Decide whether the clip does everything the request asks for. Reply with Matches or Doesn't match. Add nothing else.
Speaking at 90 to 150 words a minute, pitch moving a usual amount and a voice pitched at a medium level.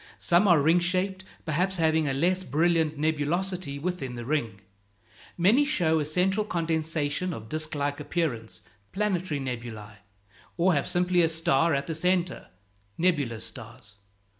Matches